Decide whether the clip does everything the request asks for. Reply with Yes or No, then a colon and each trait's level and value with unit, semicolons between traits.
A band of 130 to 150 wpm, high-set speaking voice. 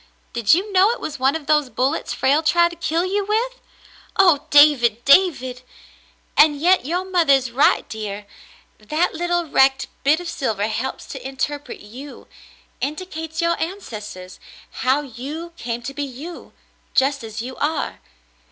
No: average, 165 wpm; very high, 290 Hz